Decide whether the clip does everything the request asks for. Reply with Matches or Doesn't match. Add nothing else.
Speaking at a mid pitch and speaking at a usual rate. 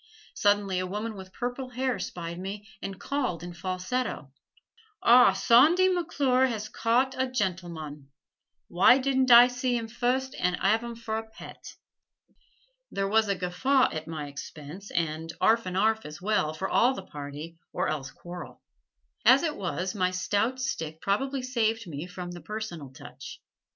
Doesn't match